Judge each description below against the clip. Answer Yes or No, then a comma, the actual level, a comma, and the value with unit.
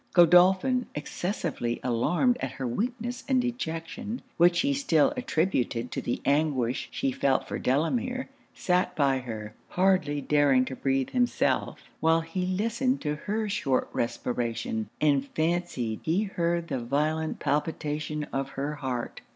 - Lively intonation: Yes, wide, 6.2 semitones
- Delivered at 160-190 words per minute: No, slow, 135 wpm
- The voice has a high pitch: No, medium, 155 Hz